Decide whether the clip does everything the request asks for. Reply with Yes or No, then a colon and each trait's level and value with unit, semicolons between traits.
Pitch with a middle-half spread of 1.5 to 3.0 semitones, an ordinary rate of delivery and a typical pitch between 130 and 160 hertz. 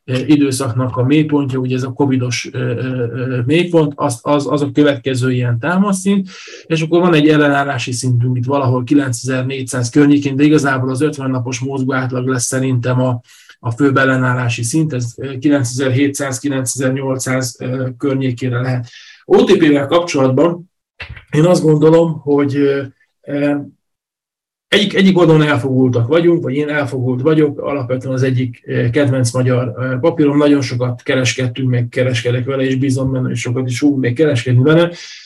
Yes: narrow, 2.4 semitones; average, 135 wpm; low, 135 Hz